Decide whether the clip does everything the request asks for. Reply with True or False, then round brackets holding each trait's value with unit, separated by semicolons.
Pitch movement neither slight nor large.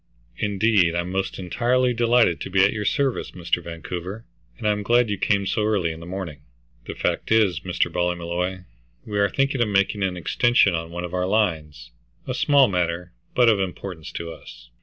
True (3.8 semitones)